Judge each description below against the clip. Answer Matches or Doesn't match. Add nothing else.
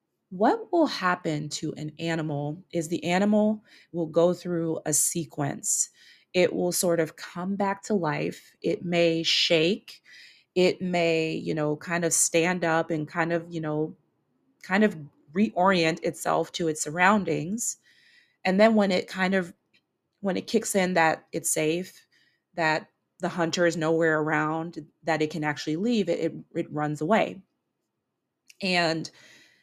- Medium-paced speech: Matches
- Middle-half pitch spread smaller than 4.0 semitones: Matches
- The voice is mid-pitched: Matches